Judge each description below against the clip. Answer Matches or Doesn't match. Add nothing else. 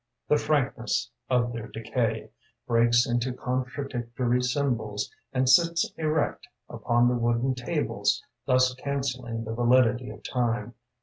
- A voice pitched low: Matches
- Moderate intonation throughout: Doesn't match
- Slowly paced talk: Matches